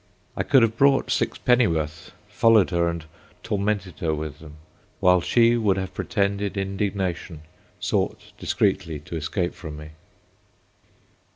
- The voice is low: Yes, very low, 95 Hz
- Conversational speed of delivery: No, slow, 125 wpm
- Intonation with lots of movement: No, average, 4.5 semitones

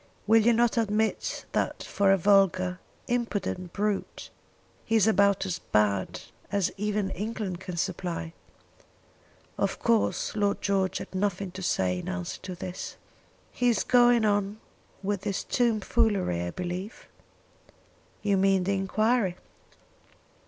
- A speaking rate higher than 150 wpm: No, slow, 135 wpm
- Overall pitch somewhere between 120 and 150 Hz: No, high, 200 Hz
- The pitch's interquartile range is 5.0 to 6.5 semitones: No, average, 2.8 semitones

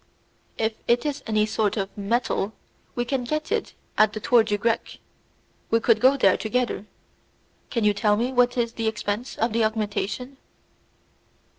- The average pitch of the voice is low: No, high, 225 Hz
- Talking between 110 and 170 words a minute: Yes, average, 165 wpm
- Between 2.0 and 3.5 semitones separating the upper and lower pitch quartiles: Yes, narrow, 2.6 semitones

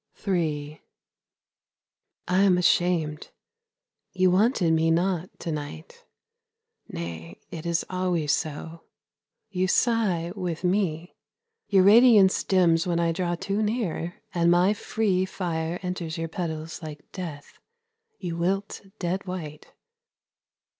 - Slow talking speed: Yes, slow, 115 wpm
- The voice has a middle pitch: Yes, medium, 175 Hz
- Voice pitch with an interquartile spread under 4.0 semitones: Yes, narrow, 2.5 semitones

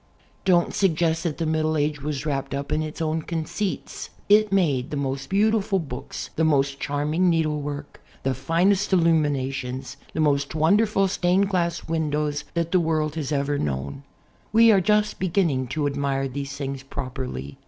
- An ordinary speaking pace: Yes, average, 160 wpm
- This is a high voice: No, medium, 155 Hz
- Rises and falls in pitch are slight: No, average, 3.8 semitones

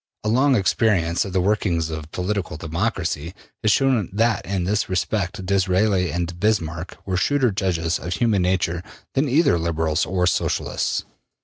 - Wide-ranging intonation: No, average, 3.9 semitones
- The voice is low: Yes, very low, 95 Hz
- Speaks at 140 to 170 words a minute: Yes, average, 150 wpm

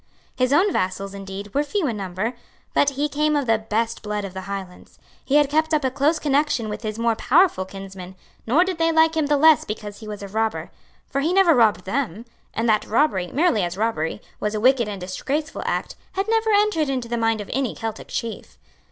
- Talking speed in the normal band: No, fast, 220 wpm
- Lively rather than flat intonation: Yes, wide, 6.3 semitones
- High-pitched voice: Yes, high, 235 Hz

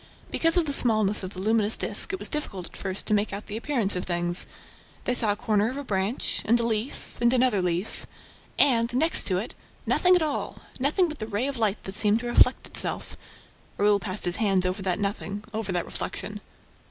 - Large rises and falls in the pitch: No, average, 4.1 semitones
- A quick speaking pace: Yes, fast, 215 wpm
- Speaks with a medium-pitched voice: No, high, 215 Hz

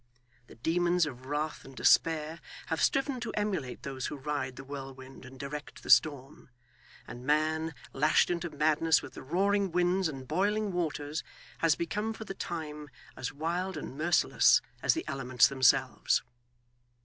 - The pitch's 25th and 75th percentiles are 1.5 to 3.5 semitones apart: No, average, 4.4 semitones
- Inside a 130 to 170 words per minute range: Yes, average, 155 wpm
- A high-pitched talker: No, medium, 155 Hz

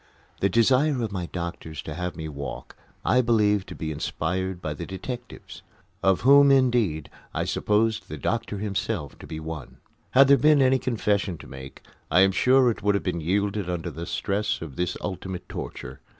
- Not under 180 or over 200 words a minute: Yes, average, 185 wpm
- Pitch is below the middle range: Yes, low, 100 Hz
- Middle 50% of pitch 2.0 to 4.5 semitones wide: No, wide, 5.6 semitones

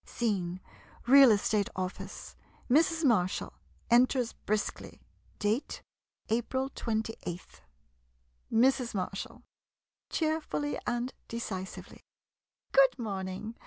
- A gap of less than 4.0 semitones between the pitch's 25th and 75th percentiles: No, average, 4.7 semitones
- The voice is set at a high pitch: Yes, high, 230 Hz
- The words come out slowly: Yes, slow, 90 wpm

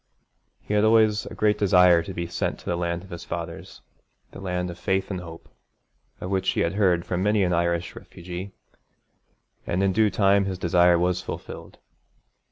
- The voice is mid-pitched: No, very low, 90 Hz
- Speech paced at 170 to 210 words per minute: Yes, average, 185 wpm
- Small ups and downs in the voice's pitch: Yes, narrow, 2.2 semitones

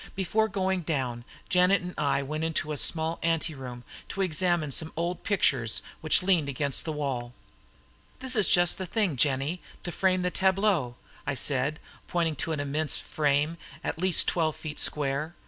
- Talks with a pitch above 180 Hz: No, medium, 160 Hz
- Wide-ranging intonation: No, average, 4.2 semitones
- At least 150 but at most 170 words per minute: Yes, average, 165 wpm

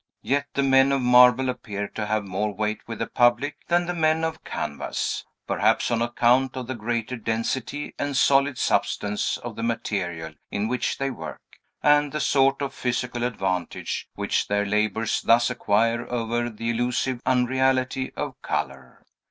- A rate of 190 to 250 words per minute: No, average, 160 wpm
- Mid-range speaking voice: No, low, 120 Hz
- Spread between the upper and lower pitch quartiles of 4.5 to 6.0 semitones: No, average, 3.5 semitones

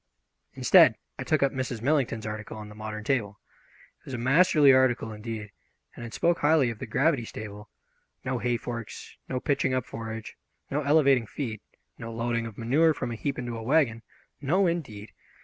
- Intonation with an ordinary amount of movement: Yes, average, 3.8 semitones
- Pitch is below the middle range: Yes, low, 120 Hz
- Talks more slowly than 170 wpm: No, average, 185 wpm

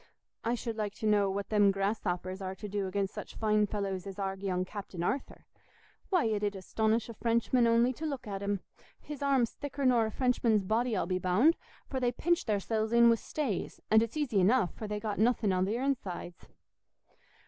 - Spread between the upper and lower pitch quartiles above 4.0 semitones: No, average, 3.5 semitones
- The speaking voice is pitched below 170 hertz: No, high, 215 Hz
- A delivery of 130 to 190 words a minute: No, fast, 205 wpm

